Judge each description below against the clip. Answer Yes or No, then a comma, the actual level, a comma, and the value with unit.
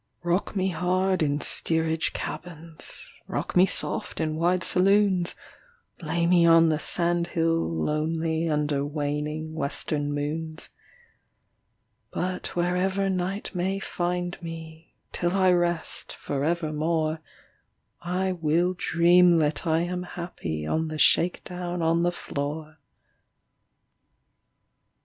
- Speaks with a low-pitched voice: No, medium, 165 Hz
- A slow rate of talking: Yes, slow, 115 wpm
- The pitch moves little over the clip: Yes, narrow, 2.3 semitones